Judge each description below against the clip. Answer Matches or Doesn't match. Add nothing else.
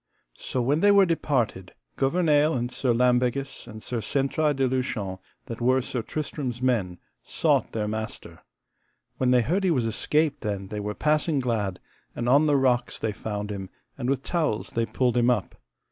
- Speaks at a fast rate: Doesn't match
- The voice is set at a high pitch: Doesn't match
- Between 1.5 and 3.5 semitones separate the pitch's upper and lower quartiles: Doesn't match